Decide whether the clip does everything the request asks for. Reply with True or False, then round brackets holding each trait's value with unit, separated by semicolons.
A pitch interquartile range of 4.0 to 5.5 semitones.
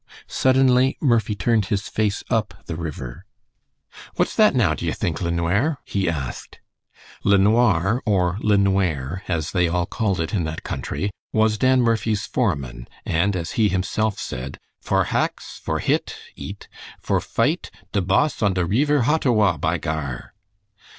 True (4.8 semitones)